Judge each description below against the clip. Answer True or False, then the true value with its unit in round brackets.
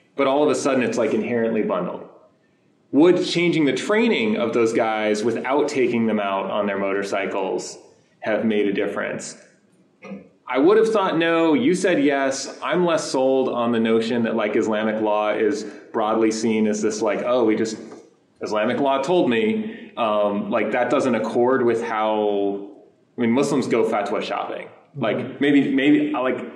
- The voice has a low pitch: True (115 Hz)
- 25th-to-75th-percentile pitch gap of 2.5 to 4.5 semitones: False (5.1 semitones)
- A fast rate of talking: False (170 wpm)